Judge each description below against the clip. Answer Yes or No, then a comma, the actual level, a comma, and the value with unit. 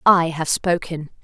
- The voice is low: No, medium, 165 Hz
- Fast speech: No, average, 145 wpm